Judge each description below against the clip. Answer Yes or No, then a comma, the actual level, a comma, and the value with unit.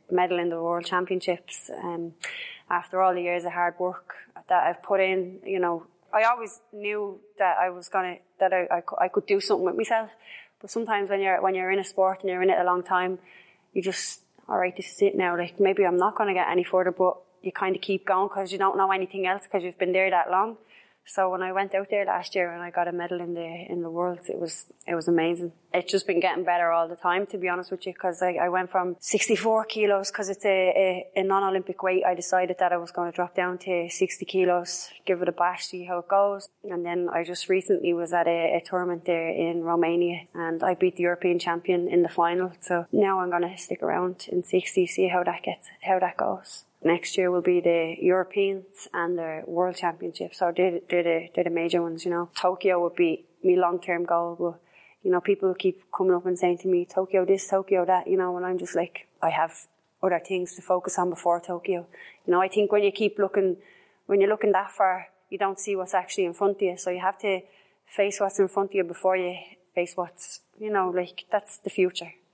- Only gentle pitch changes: Yes, narrow, 1.7 semitones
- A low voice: No, medium, 185 Hz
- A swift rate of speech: Yes, fast, 245 wpm